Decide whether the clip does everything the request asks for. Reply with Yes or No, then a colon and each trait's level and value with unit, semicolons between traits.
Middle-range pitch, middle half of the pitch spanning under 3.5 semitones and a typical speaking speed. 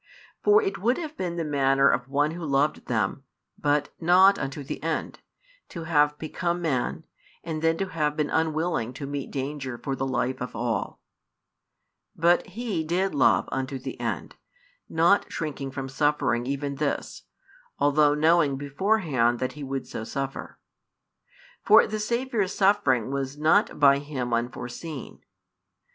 No: medium, 145 Hz; average, 4.1 semitones; average, 150 wpm